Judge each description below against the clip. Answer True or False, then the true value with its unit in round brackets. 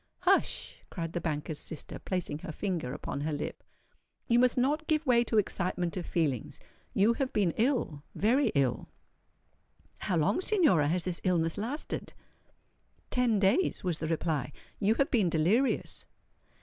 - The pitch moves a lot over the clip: True (7.1 semitones)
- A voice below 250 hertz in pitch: True (185 Hz)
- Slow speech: False (150 wpm)